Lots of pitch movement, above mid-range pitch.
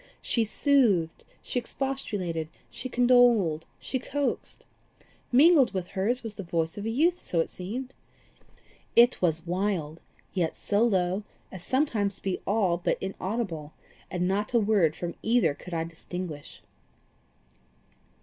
Yes: wide, 5.7 semitones; high, 200 Hz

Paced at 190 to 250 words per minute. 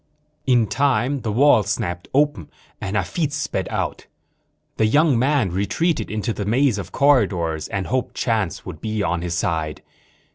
No: average, 155 wpm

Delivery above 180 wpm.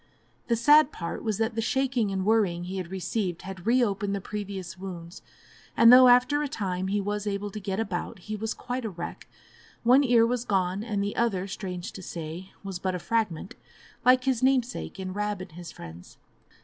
Yes: average, 200 wpm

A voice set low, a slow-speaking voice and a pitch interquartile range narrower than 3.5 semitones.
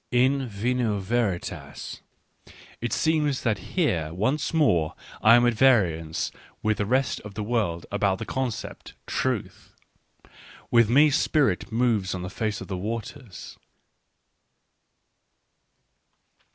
No: low, 115 Hz; slow, 130 wpm; average, 4.8 semitones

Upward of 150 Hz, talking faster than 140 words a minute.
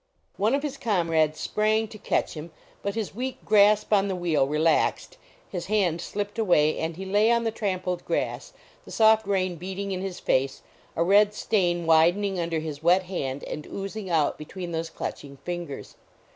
Yes: medium, 185 Hz; average, 180 wpm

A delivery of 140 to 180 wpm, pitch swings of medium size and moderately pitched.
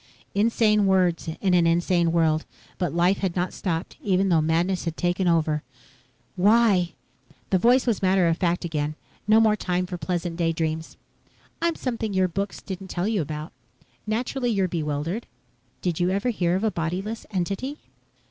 Yes: average, 165 wpm; average, 3.3 semitones; medium, 180 Hz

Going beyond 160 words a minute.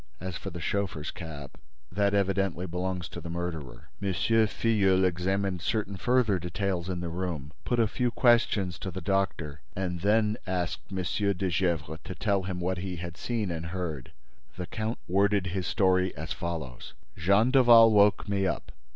Yes: average, 170 wpm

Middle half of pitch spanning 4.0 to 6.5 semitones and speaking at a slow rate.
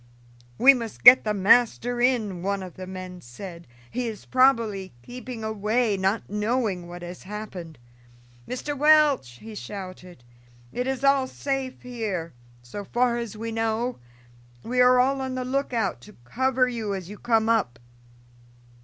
No: average, 4.7 semitones; average, 155 wpm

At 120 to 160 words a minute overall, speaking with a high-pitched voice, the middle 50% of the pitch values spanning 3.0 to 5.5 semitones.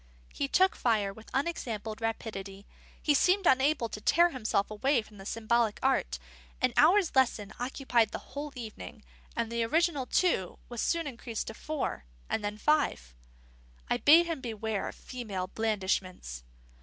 Yes: average, 155 wpm; high, 230 Hz; average, 5.2 semitones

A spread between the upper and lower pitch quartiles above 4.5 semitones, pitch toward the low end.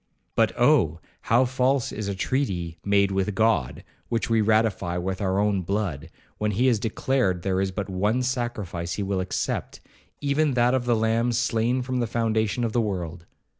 No: average, 4.1 semitones; low, 110 Hz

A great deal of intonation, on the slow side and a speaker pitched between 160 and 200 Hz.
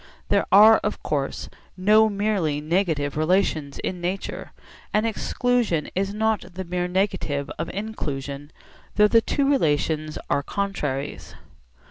Yes: wide, 5.7 semitones; slow, 125 wpm; medium, 185 Hz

